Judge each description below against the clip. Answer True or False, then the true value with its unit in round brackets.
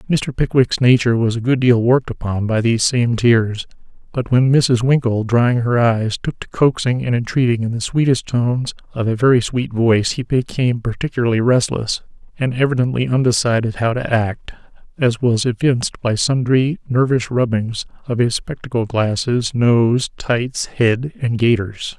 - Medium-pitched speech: False (120 Hz)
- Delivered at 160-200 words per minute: True (165 wpm)